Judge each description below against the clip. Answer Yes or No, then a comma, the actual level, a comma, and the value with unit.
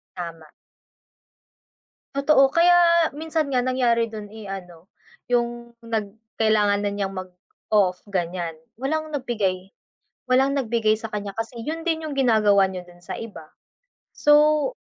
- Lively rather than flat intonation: Yes, wide, 6.0 semitones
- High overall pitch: Yes, high, 225 Hz